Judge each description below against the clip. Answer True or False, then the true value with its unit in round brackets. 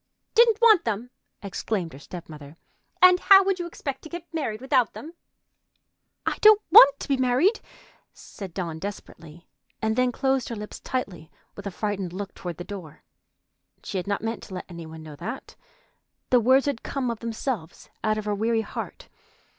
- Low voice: False (225 Hz)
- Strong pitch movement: True (6.8 semitones)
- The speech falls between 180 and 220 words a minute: True (185 wpm)